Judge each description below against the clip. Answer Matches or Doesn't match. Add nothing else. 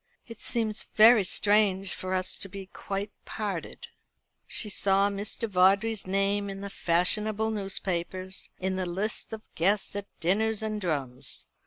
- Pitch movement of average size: Doesn't match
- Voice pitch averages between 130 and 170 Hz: Doesn't match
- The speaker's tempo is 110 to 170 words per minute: Matches